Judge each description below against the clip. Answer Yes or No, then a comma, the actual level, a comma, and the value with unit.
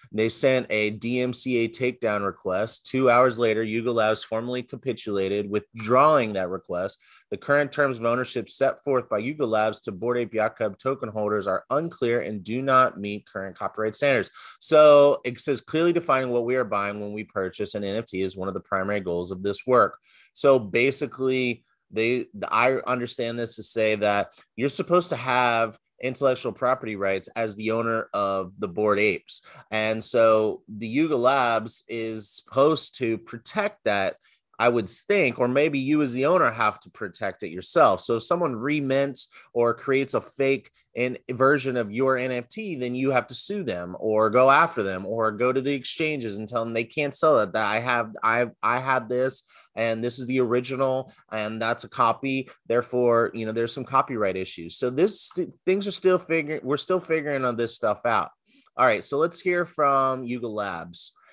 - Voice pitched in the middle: No, low, 120 Hz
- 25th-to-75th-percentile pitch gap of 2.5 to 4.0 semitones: Yes, average, 3.6 semitones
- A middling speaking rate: Yes, average, 185 wpm